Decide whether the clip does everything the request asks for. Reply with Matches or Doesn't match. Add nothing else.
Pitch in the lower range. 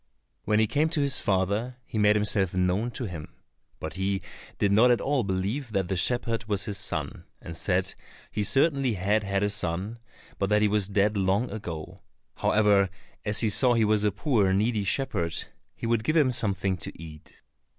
Matches